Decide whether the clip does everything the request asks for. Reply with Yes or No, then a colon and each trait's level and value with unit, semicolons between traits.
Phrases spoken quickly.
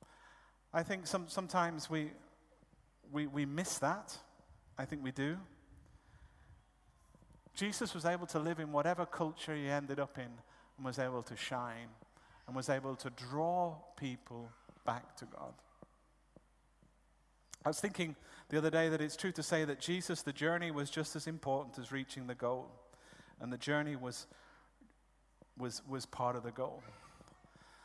No: average, 155 wpm